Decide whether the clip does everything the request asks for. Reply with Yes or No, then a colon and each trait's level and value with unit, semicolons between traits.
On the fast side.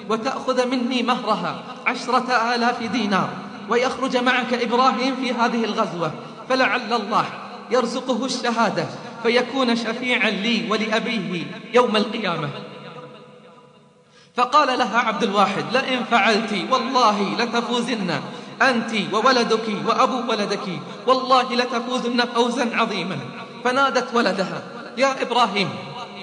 No: average, 95 wpm